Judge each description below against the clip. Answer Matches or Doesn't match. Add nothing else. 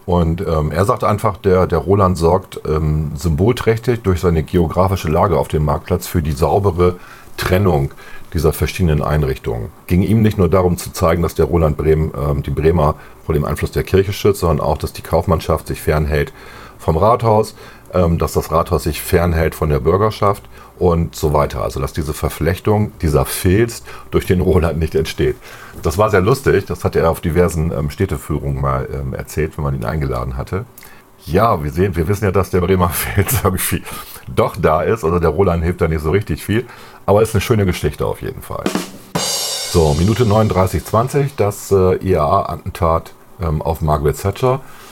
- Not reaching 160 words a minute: Doesn't match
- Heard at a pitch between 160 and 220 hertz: Doesn't match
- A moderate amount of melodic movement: Matches